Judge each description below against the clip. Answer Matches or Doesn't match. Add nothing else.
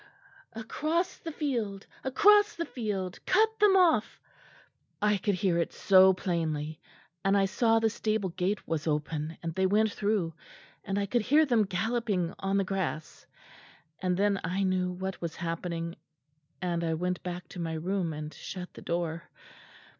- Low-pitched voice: Doesn't match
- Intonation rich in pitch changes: Doesn't match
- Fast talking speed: Doesn't match